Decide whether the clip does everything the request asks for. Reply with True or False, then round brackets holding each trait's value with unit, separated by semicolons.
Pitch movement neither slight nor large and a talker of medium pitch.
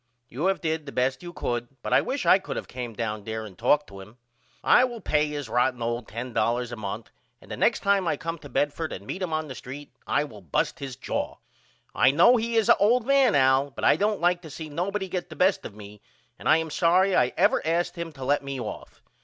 False (6.6 semitones; 145 Hz)